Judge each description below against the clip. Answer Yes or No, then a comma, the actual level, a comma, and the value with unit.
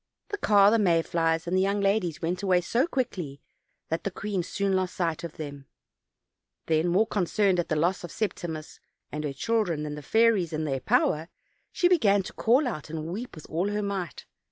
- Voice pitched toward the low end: No, medium, 180 Hz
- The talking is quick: Yes, fast, 210 wpm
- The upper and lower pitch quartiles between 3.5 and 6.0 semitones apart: Yes, average, 4.2 semitones